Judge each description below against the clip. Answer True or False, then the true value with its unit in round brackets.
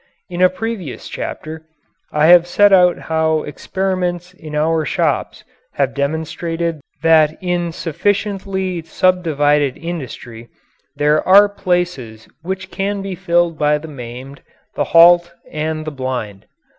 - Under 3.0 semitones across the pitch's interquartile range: False (3.4 semitones)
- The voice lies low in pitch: False (165 Hz)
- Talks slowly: True (125 wpm)